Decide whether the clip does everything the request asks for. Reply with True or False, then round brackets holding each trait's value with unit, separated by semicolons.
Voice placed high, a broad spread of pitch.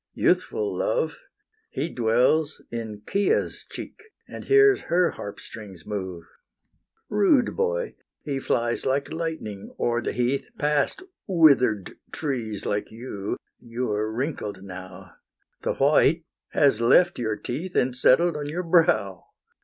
False (130 Hz; 7.7 semitones)